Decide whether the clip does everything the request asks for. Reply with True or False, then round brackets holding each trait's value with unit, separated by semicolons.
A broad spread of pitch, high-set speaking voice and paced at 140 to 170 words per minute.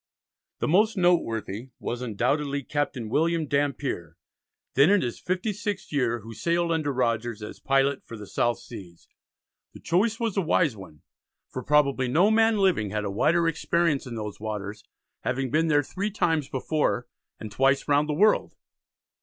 False (6.4 semitones; 140 Hz; 165 wpm)